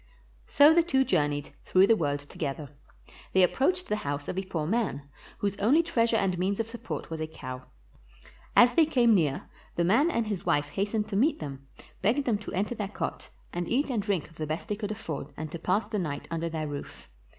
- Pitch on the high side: Yes, high, 195 Hz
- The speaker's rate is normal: No, fast, 215 wpm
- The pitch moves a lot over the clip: Yes, wide, 6.6 semitones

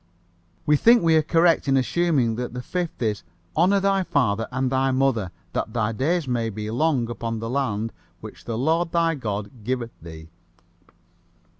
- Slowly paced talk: No, average, 170 wpm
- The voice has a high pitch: No, low, 130 Hz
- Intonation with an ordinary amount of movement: No, wide, 6.3 semitones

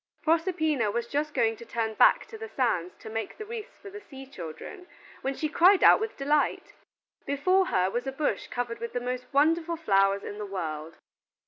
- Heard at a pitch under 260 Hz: No, very high, 270 Hz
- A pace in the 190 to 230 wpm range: Yes, average, 200 wpm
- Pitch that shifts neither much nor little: No, wide, 7.0 semitones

